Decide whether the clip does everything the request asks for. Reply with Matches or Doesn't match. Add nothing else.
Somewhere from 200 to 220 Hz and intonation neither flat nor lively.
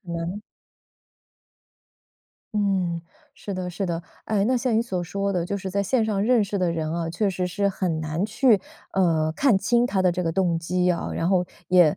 Doesn't match